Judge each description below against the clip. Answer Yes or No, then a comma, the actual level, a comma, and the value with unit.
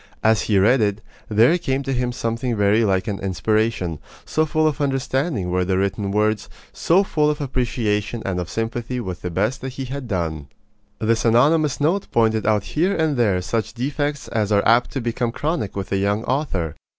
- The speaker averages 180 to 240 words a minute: Yes, average, 195 wpm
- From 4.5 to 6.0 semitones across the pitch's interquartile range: Yes, average, 4.9 semitones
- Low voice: Yes, low, 115 Hz